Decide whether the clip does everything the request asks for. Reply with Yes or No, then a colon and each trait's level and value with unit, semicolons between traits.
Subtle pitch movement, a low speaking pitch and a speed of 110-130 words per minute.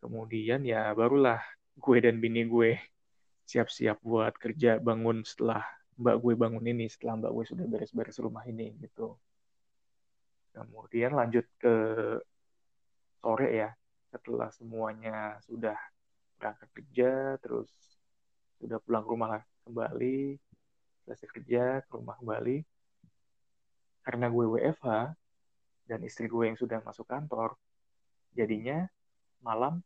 Yes: narrow, 1.8 semitones; low, 115 Hz; average, 115 wpm